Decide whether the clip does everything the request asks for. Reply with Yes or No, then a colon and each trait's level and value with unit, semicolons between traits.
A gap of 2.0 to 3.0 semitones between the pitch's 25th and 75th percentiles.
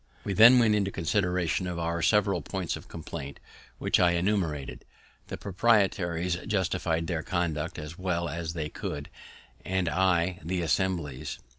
Yes: narrow, 2.5 semitones